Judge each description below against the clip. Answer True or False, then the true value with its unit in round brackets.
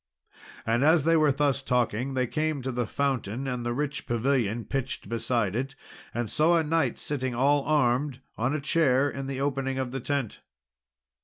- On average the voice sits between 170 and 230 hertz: False (135 Hz)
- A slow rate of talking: False (180 wpm)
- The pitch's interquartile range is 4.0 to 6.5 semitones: False (2.8 semitones)